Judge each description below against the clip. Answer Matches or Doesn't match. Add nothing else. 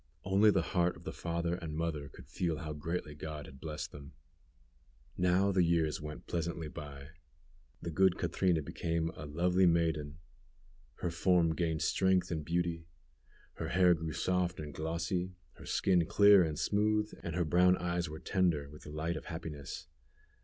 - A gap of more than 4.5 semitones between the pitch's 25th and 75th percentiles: Doesn't match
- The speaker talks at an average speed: Matches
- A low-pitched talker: Matches